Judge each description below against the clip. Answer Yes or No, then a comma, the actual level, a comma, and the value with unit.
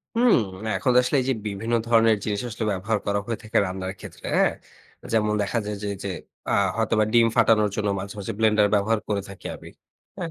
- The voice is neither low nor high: No, low, 105 Hz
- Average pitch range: No, narrow, 2.0 semitones